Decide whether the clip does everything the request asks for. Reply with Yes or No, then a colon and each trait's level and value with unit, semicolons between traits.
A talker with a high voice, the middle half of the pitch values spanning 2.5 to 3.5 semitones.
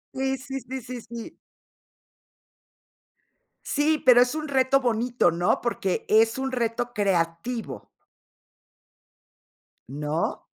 No: high, 240 Hz; average, 3.9 semitones